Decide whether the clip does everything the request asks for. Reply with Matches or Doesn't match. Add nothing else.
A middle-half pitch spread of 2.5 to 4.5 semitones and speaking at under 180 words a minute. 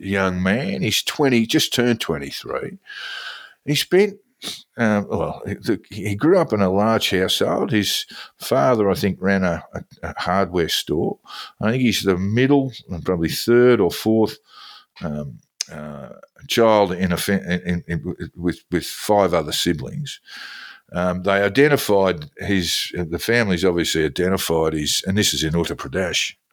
Doesn't match